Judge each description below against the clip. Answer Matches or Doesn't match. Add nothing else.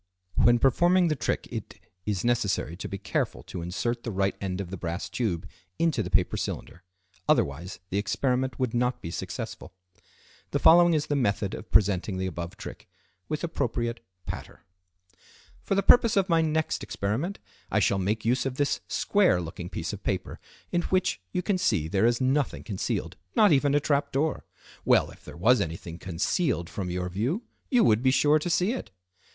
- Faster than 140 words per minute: Matches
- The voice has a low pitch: Matches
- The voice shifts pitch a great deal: Matches